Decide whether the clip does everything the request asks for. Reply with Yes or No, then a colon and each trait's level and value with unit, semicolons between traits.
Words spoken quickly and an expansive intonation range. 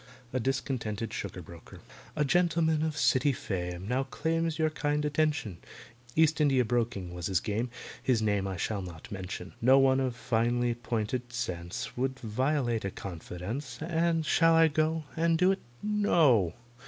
No: average, 155 wpm; wide, 6.5 semitones